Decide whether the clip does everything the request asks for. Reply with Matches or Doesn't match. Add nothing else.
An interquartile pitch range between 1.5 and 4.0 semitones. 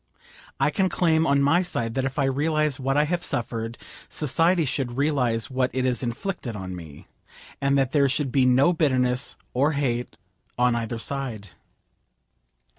Matches